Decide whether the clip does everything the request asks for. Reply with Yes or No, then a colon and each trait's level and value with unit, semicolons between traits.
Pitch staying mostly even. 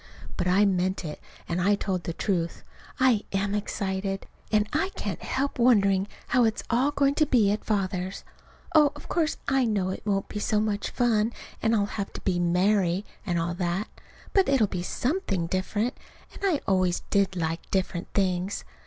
No: average, 3.7 semitones